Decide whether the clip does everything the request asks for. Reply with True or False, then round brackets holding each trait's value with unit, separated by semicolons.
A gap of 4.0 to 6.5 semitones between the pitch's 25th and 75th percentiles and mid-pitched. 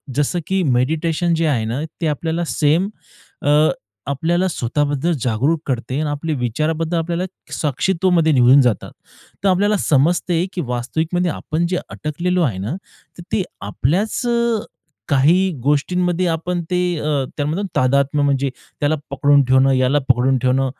True (4.3 semitones; 150 Hz)